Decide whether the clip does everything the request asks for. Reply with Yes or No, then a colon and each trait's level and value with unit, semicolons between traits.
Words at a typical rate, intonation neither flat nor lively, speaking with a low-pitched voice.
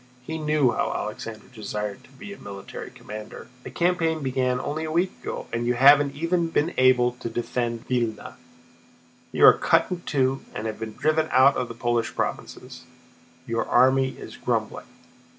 Yes: average, 170 wpm; average, 4.7 semitones; low, 130 Hz